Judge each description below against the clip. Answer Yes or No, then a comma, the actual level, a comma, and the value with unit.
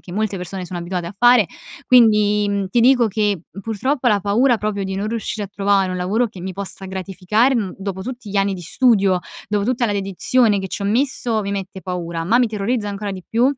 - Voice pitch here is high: Yes, high, 205 Hz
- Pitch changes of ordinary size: Yes, average, 3.1 semitones